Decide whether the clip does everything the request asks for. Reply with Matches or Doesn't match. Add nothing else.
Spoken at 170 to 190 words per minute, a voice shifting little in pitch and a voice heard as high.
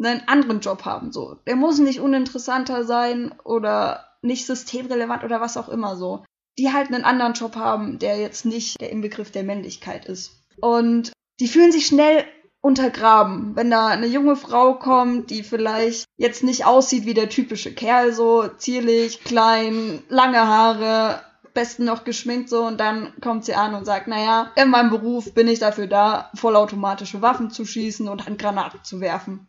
Matches